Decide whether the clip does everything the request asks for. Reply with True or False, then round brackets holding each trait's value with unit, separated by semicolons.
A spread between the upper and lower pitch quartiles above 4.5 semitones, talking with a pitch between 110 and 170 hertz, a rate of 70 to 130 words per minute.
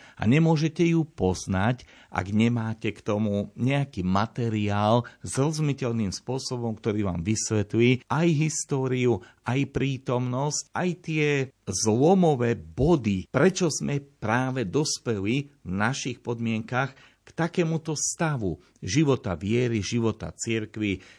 True (4.9 semitones; 120 Hz; 110 wpm)